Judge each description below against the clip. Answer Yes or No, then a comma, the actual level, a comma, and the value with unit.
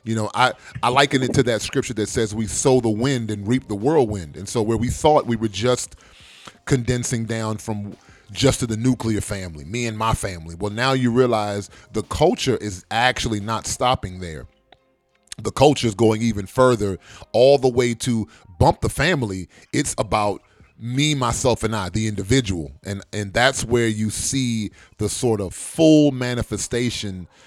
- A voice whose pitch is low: Yes, low, 115 Hz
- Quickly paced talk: No, average, 180 wpm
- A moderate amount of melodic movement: Yes, average, 3.4 semitones